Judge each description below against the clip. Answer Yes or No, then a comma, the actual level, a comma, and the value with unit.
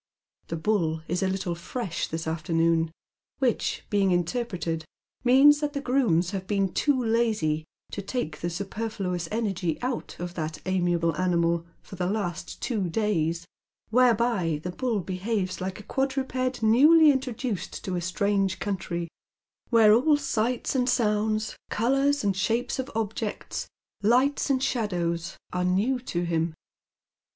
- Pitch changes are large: Yes, wide, 5.8 semitones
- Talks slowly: No, average, 145 wpm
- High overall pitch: Yes, high, 200 Hz